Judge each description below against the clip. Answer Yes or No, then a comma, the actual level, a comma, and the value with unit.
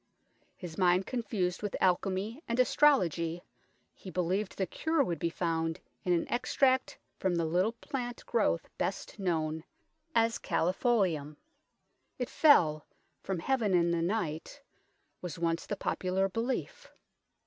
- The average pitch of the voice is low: No, medium, 185 Hz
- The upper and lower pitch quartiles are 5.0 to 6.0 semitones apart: Yes, wide, 5.4 semitones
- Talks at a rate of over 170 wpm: No, slow, 135 wpm